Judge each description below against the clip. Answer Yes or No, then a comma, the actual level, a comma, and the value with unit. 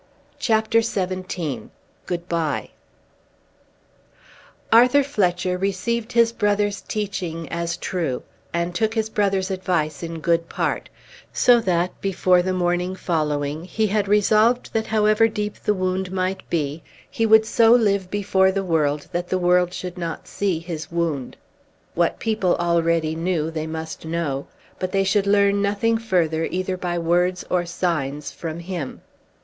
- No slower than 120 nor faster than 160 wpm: Yes, average, 145 wpm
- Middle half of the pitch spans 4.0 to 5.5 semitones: No, average, 3.5 semitones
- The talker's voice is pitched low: No, medium, 185 Hz